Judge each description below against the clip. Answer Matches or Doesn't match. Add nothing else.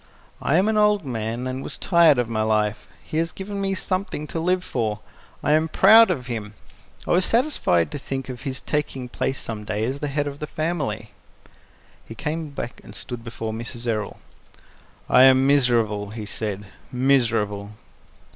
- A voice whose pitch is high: Doesn't match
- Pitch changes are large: Matches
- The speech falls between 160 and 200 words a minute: Matches